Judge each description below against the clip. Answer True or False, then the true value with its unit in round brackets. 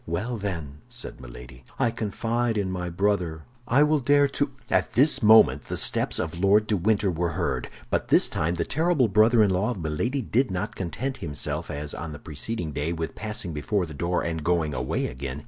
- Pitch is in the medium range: False (95 Hz)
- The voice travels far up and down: True (6.2 semitones)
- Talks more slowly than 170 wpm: False (200 wpm)